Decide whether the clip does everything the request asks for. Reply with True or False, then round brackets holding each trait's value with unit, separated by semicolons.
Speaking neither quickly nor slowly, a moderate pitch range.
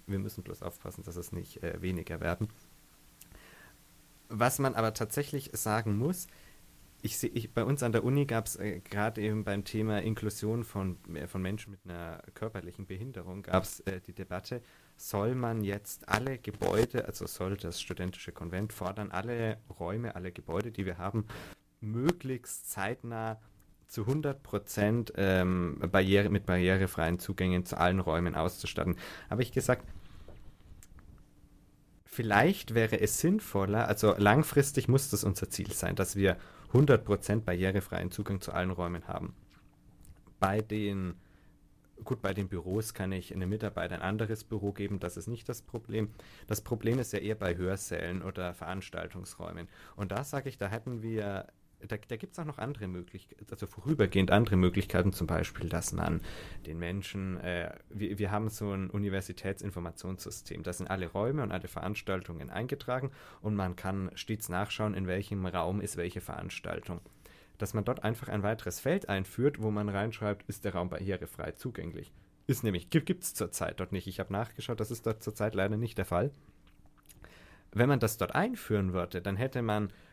True (165 wpm; 3.4 semitones)